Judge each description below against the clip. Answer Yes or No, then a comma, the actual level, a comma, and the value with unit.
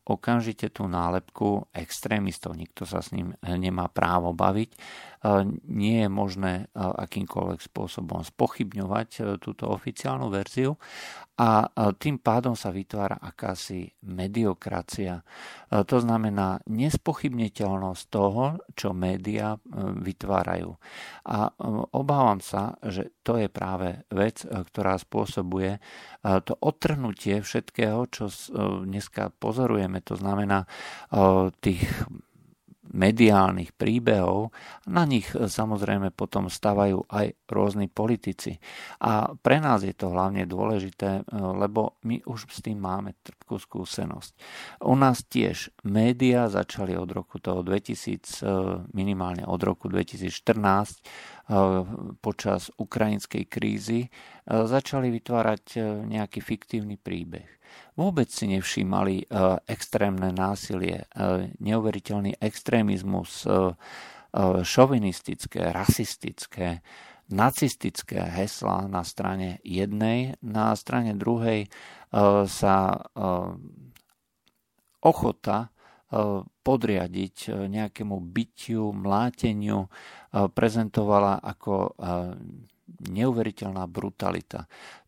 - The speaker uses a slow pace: Yes, slow, 90 wpm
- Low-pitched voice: Yes, low, 100 Hz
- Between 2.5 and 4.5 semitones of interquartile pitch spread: Yes, average, 2.9 semitones